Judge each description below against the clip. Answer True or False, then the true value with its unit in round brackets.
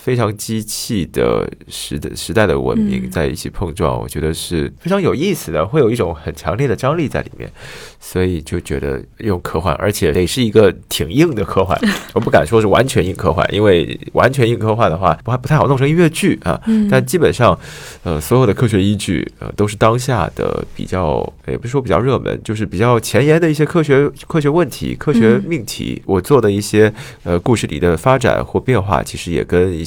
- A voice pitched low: True (110 Hz)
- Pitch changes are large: True (6.9 semitones)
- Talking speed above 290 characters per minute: True (315 characters per minute)